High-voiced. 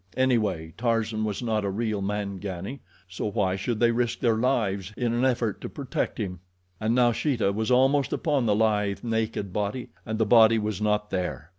No: low, 110 Hz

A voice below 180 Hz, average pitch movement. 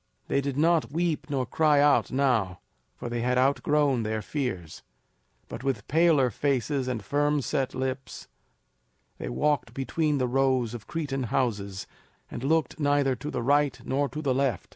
Yes: low, 135 Hz; average, 3.1 semitones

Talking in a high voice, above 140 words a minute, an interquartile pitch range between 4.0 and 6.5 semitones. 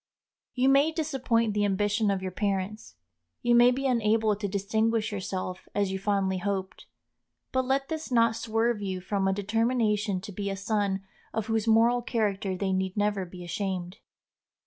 No: high, 210 Hz; average, 170 wpm; average, 3.0 semitones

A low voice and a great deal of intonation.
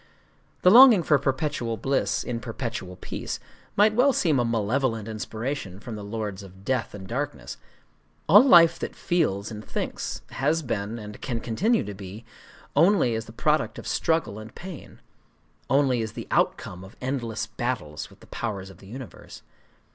Yes: low, 115 Hz; wide, 6.1 semitones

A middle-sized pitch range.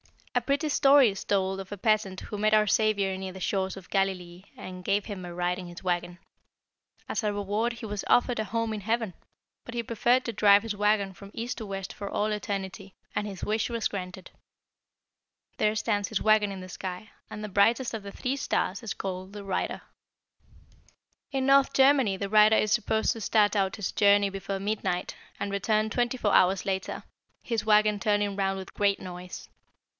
No: narrow, 2.2 semitones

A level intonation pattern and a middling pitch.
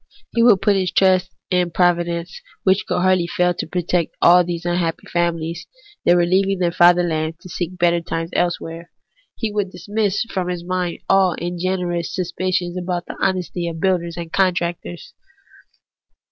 Yes: narrow, 1.4 semitones; medium, 175 Hz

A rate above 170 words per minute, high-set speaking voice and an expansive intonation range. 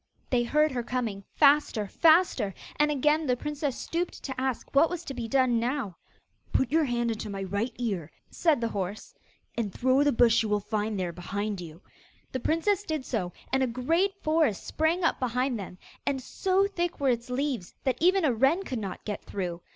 Yes: average, 195 wpm; very high, 255 Hz; wide, 5.9 semitones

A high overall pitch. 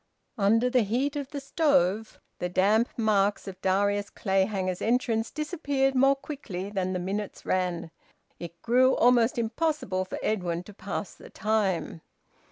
Yes: high, 210 Hz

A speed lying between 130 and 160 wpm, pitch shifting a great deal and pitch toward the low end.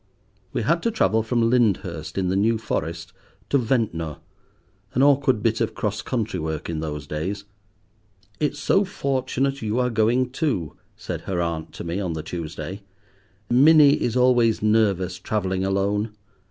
Yes: average, 155 wpm; wide, 5.8 semitones; low, 110 Hz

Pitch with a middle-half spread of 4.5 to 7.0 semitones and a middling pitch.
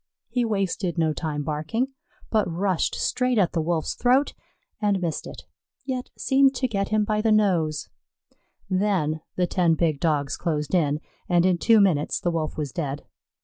Yes: average, 5.3 semitones; medium, 180 Hz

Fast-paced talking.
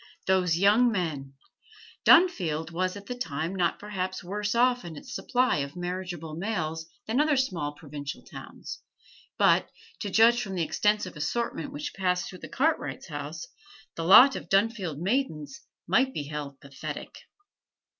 No: average, 145 wpm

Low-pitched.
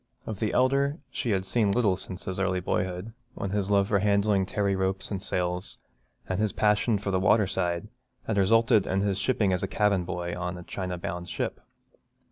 Yes: very low, 95 Hz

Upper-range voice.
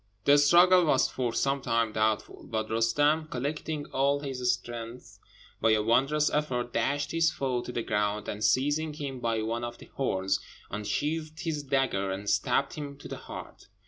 No: low, 130 Hz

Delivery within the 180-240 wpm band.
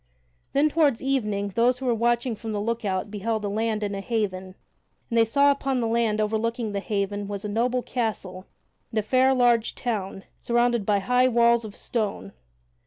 Yes: average, 185 wpm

